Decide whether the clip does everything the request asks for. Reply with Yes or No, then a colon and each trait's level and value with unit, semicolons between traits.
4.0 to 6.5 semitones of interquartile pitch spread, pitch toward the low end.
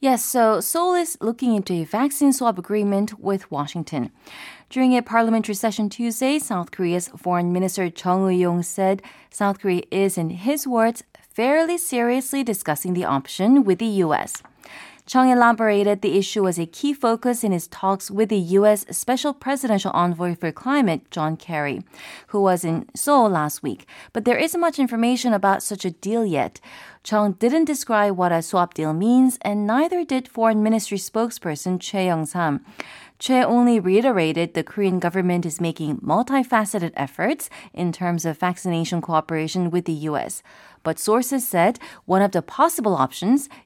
No: wide, 5.5 semitones; high, 205 Hz